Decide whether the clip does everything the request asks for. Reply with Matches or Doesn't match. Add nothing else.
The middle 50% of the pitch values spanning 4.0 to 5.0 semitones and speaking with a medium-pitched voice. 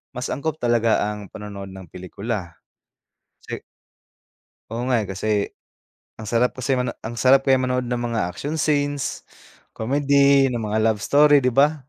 Doesn't match